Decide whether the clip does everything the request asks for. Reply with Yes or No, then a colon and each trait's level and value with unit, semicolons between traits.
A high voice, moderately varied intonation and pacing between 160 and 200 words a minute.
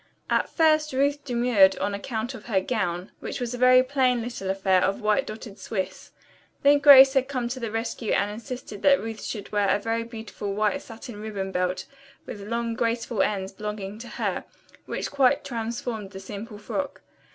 Yes: high, 225 Hz; average, 3.8 semitones; average, 185 wpm